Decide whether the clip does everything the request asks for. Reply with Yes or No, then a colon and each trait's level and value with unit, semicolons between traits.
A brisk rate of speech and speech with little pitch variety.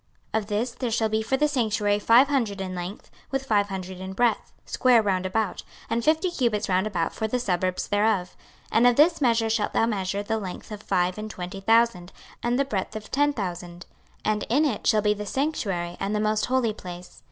No: fast, 220 wpm; average, 3.8 semitones